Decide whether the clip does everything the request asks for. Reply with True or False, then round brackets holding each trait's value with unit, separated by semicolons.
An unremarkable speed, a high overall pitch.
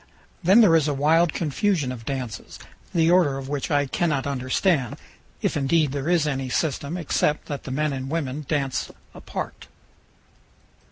False (160 wpm; 145 Hz)